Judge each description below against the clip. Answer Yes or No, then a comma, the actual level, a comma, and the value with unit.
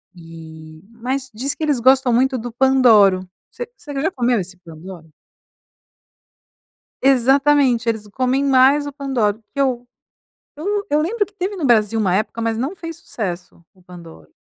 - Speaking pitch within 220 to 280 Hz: Yes, high, 245 Hz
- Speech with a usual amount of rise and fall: No, wide, 5.9 semitones